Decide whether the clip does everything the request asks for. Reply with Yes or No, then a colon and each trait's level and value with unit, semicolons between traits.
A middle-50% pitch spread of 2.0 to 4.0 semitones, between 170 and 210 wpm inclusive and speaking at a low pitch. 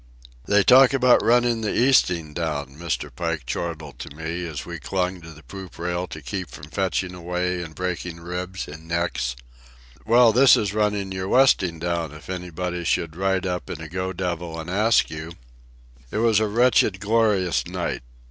Yes: average, 3.5 semitones; average, 175 wpm; very low, 90 Hz